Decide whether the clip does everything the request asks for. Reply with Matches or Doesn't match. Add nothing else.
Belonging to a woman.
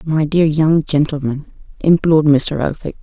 Matches